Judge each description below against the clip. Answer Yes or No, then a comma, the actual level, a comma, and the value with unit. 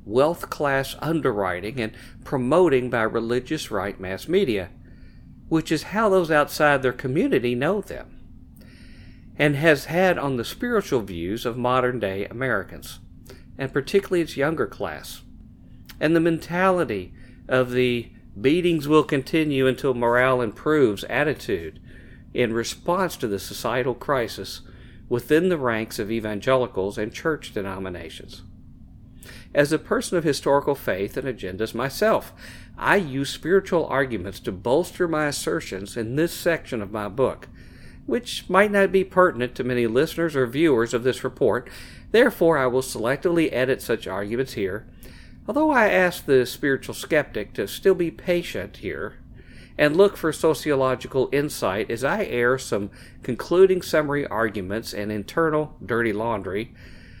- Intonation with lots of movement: Yes, wide, 5.9 semitones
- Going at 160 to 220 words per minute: No, average, 140 wpm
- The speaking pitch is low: Yes, low, 130 Hz